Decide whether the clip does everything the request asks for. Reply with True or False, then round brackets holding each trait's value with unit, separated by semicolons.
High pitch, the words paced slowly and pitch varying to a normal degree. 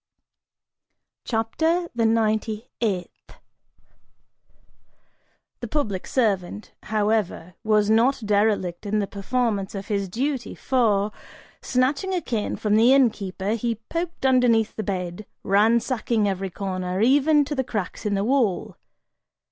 True (220 Hz; 120 wpm; 3.9 semitones)